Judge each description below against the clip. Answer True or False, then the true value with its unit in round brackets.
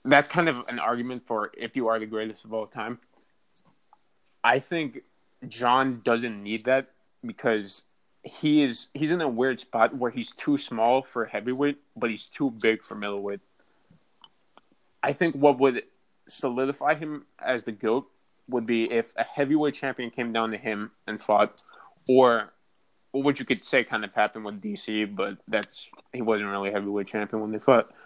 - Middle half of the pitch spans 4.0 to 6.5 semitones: True (4.6 semitones)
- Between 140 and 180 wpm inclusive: True (175 wpm)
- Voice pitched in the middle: False (120 Hz)